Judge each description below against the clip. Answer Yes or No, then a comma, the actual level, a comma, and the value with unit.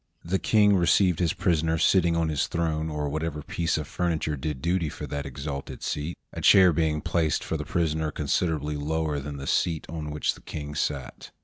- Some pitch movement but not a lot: No, narrow, 2.2 semitones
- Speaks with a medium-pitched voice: No, very low, 80 Hz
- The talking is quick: No, average, 195 wpm